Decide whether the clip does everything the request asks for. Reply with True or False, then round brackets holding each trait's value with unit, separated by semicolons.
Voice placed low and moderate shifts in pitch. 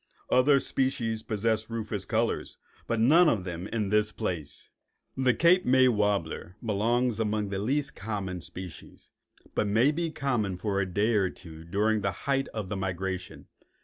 True (105 Hz; 4.1 semitones)